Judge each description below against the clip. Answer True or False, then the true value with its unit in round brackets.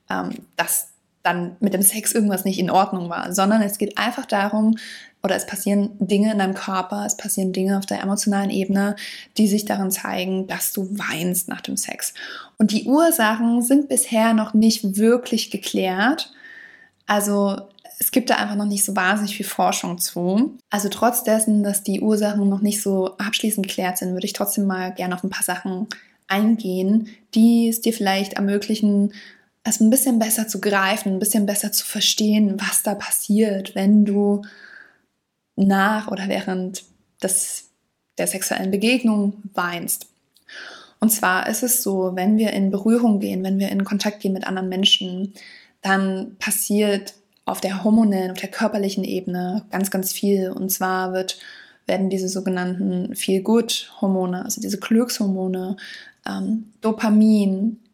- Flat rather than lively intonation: True (2.3 semitones)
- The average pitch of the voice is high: True (205 Hz)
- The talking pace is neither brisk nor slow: True (160 wpm)